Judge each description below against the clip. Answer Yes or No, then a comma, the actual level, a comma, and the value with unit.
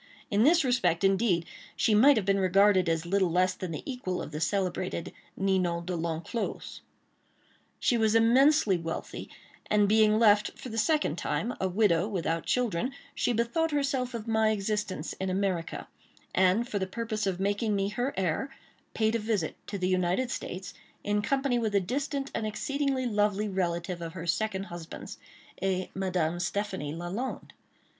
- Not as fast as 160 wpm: No, average, 165 wpm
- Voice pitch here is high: Yes, high, 200 Hz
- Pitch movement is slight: No, average, 4.1 semitones